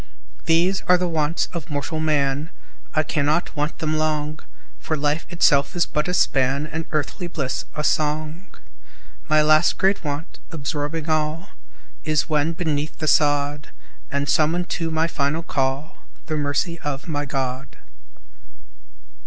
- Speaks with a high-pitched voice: No, medium, 155 Hz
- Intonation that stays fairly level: Yes, narrow, 2.0 semitones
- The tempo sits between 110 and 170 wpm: Yes, average, 145 wpm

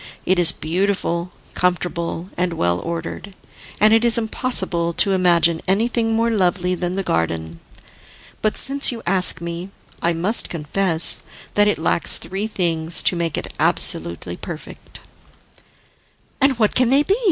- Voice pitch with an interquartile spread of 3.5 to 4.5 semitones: Yes, average, 4.0 semitones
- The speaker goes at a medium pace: Yes, average, 145 wpm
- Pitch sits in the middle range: Yes, medium, 180 Hz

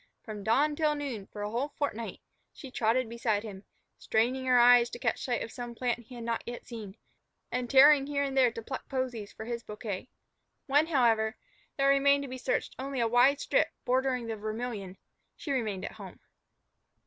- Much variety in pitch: No, average, 3.4 semitones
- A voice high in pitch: Yes, high, 245 Hz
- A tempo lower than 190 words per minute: No, average, 195 wpm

